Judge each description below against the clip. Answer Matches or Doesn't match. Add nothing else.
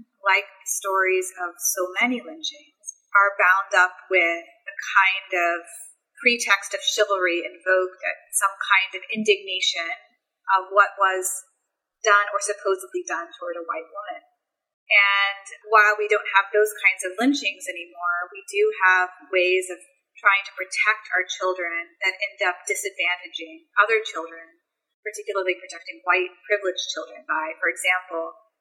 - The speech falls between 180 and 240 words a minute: Doesn't match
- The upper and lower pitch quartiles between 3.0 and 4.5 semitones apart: Doesn't match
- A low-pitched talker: Doesn't match